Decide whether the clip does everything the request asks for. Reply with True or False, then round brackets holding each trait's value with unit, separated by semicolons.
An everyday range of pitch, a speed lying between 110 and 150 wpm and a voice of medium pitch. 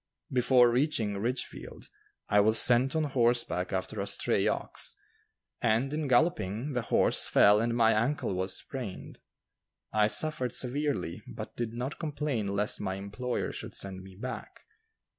False (4.4 semitones; 145 wpm; 120 Hz)